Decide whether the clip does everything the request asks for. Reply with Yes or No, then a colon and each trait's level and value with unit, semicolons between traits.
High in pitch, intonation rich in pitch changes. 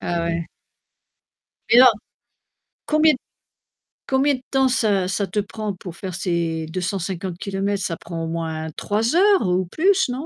Yes: high, 195 Hz; wide, 6.7 semitones